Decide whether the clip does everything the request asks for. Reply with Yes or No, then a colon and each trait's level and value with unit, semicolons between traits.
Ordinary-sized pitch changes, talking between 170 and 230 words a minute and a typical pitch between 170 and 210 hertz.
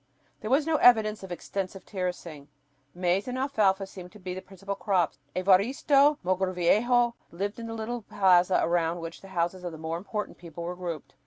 Yes: average, 3.5 semitones; average, 180 wpm; high, 190 Hz